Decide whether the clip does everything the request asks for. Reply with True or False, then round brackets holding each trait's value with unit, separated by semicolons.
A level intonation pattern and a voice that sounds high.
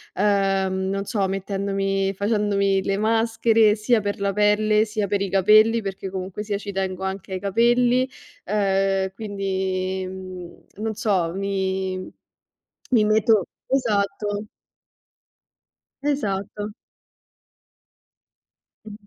True (1.8 semitones; 200 Hz)